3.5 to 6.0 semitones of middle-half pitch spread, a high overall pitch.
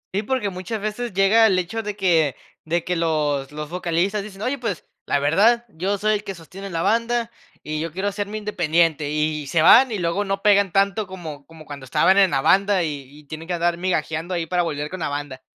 No: average, 4.5 semitones; medium, 180 Hz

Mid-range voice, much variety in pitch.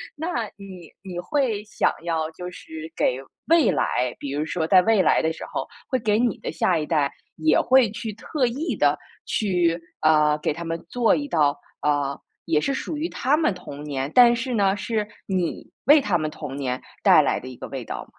Yes: medium, 180 Hz; wide, 7.3 semitones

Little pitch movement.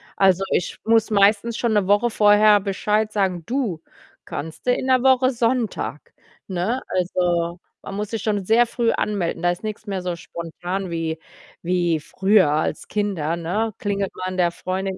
No: average, 3.7 semitones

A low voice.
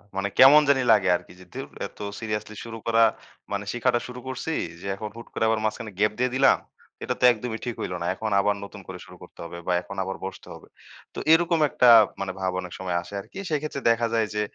Yes: low, 110 Hz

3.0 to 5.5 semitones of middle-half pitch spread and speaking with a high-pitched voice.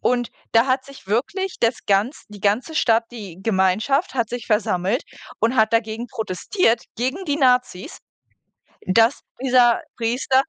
Yes: average, 3.3 semitones; high, 235 Hz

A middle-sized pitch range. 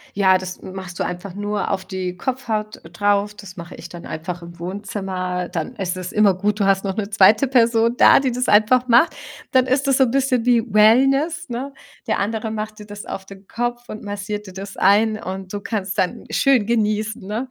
Yes: average, 3.7 semitones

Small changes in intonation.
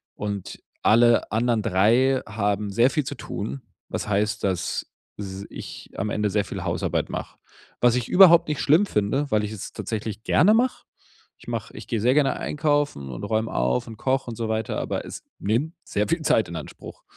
No: average, 4.7 semitones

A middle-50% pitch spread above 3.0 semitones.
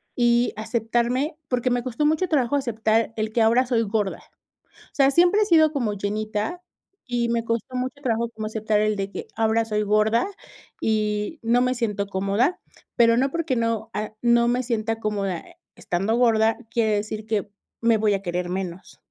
No: narrow, 2.5 semitones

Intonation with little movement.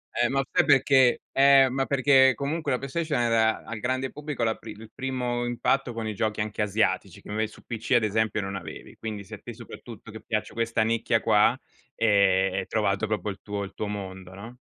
No: average, 3.6 semitones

